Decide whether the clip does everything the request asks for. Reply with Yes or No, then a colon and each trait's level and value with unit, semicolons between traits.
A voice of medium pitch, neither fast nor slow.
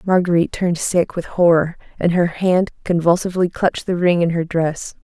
Yes: medium, 175 Hz; average, 175 wpm